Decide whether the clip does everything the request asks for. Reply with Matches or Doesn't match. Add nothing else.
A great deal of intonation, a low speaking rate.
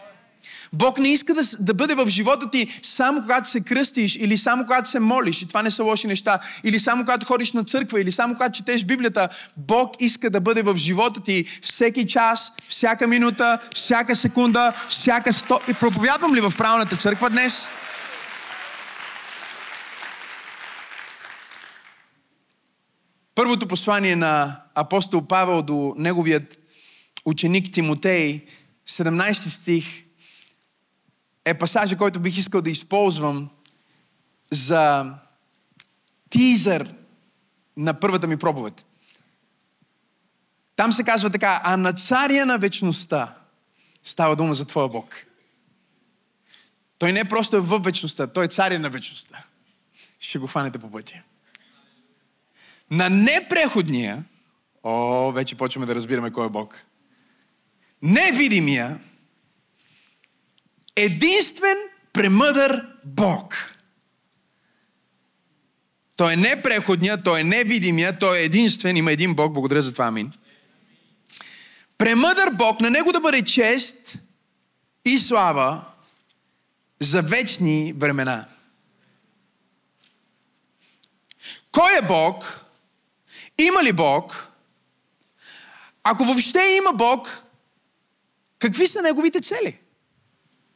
Matches